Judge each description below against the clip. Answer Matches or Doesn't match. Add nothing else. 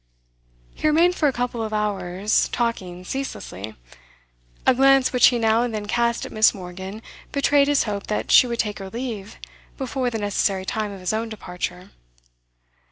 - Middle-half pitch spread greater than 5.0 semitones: Doesn't match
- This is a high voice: Matches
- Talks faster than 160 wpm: Matches